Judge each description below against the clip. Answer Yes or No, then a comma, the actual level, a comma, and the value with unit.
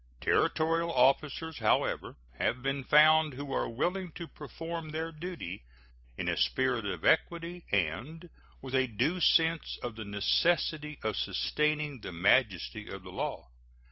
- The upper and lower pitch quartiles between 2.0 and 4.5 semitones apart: No, average, 5.2 semitones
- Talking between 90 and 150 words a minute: Yes, average, 140 wpm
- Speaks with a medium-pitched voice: Yes, medium, 150 Hz